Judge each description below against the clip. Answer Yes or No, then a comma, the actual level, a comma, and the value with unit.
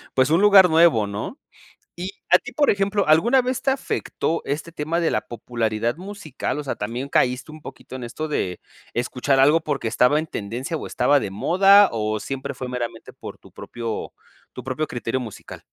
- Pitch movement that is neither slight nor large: No, wide, 5.9 semitones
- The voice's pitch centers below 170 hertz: Yes, medium, 140 Hz